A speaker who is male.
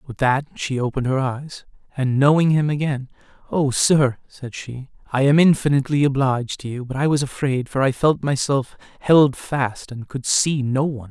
Yes: male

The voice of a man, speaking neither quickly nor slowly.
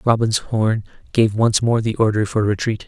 Yes: male; average, 190 wpm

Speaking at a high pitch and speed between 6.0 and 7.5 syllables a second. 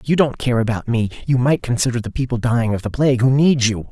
No: low, 125 Hz; 6.5 syllables/s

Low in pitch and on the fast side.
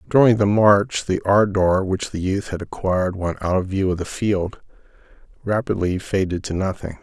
No: very low, 95 Hz; average, 180 wpm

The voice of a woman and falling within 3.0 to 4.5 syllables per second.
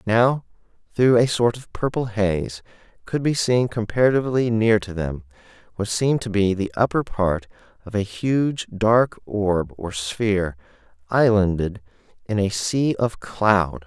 No: male; 4.2 syllables/s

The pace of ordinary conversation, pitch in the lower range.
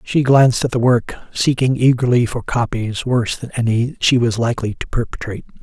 Yes: average, 180 wpm; low, 120 Hz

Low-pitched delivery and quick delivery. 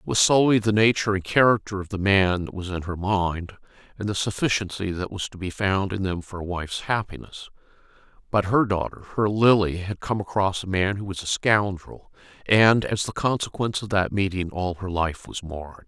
Yes: low, 100 Hz; fast, 210 wpm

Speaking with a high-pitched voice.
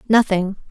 Yes: high, 200 Hz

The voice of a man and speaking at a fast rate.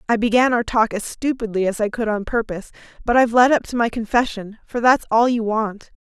No: female; fast, 230 wpm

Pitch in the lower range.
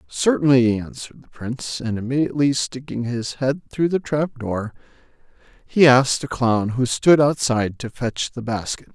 Yes: low, 125 Hz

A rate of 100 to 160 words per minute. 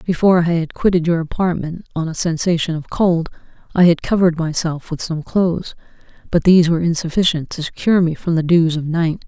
No: average, 195 wpm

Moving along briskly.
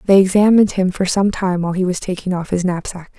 Yes: fast, 245 wpm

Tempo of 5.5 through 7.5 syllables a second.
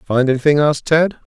Yes: 6.3 syllables/s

